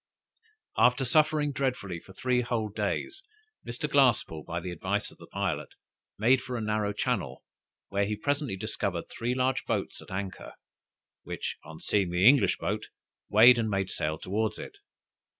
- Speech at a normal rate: Yes, average, 160 wpm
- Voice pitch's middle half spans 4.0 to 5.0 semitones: Yes, average, 4.7 semitones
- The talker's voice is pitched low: Yes, low, 110 Hz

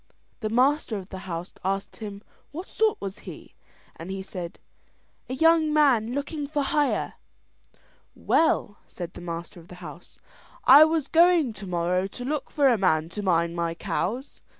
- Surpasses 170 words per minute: No, average, 165 wpm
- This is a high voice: Yes, high, 210 Hz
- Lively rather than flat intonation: Yes, wide, 8.4 semitones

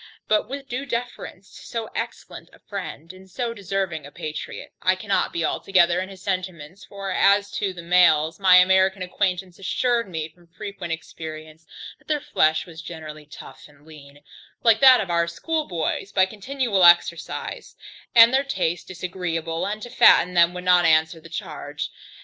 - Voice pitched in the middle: Yes, medium, 180 Hz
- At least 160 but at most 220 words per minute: Yes, average, 170 wpm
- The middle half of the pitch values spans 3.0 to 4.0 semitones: Yes, average, 3.4 semitones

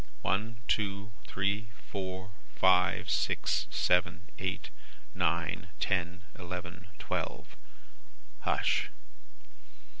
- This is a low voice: Yes, very low, 95 Hz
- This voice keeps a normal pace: No, slow, 80 wpm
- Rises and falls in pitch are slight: Yes, narrow, 2.0 semitones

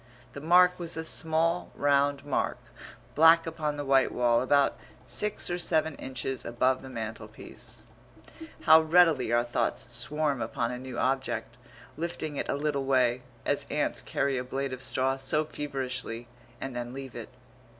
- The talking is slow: No, average, 160 wpm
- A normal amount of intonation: Yes, average, 3.6 semitones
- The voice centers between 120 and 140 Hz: Yes, low, 135 Hz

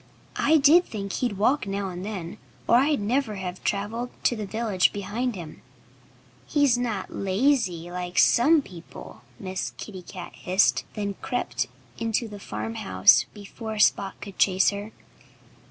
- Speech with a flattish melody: No, average, 4.1 semitones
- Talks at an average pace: Yes, average, 150 wpm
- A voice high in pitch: Yes, high, 205 Hz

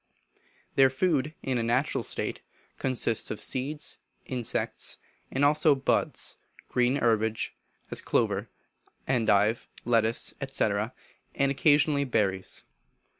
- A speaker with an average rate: No, slow, 105 wpm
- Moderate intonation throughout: Yes, average, 3.7 semitones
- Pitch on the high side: No, low, 130 Hz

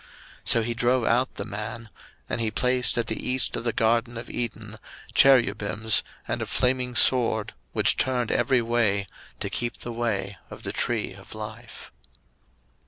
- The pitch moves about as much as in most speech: No, narrow, 2.1 semitones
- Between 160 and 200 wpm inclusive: Yes, average, 170 wpm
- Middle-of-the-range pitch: No, low, 115 Hz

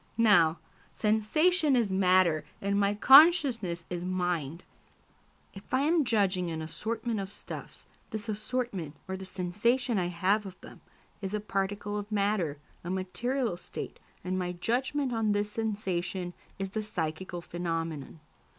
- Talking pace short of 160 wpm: Yes, average, 140 wpm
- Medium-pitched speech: No, high, 200 Hz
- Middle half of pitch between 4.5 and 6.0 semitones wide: No, average, 3.9 semitones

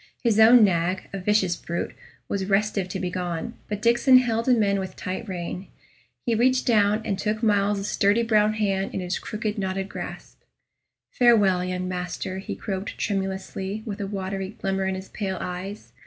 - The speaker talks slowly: No, average, 175 wpm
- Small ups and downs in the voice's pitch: Yes, narrow, 2.2 semitones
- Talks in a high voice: Yes, high, 195 Hz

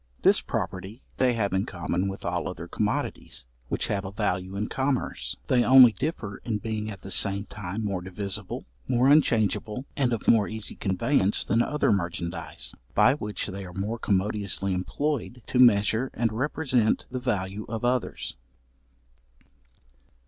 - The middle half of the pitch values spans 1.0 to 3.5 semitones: No, average, 4.0 semitones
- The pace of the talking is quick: No, average, 155 wpm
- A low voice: Yes, low, 105 Hz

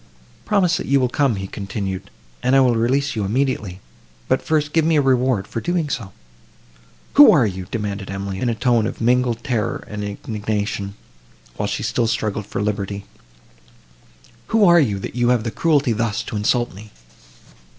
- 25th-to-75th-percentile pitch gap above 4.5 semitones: Yes, average, 4.9 semitones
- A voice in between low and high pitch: No, low, 115 Hz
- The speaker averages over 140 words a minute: Yes, average, 170 wpm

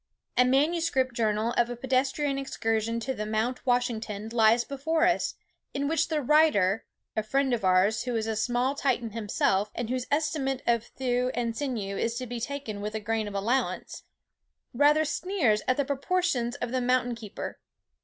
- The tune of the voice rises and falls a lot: No, average, 3.8 semitones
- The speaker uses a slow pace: No, average, 175 wpm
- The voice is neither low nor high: No, high, 245 Hz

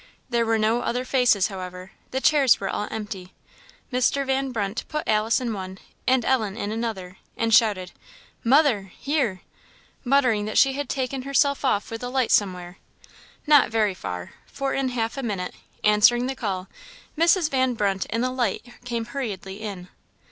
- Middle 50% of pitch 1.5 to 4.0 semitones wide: No, average, 4.6 semitones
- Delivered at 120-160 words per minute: No, average, 170 wpm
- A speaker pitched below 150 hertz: No, high, 230 Hz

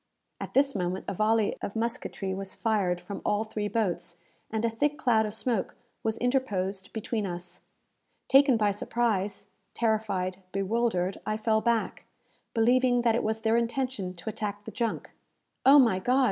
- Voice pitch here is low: No, high, 220 Hz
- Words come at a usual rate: Yes, average, 160 wpm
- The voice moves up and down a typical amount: Yes, average, 3.3 semitones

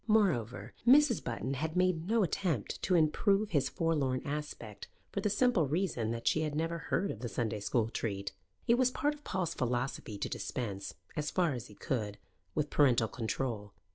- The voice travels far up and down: Yes, wide, 7.8 semitones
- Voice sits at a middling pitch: Yes, medium, 145 Hz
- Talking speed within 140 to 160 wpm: No, average, 180 wpm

